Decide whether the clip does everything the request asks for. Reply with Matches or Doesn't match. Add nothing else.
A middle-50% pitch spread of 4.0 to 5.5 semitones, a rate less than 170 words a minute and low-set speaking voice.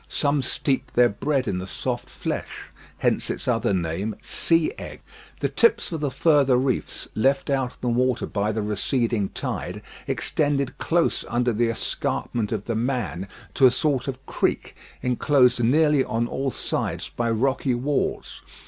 Doesn't match